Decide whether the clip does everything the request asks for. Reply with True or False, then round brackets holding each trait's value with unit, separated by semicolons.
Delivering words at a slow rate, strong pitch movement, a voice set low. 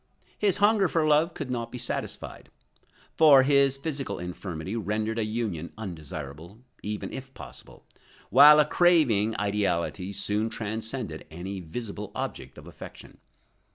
True (130 wpm; 6.1 semitones; 110 Hz)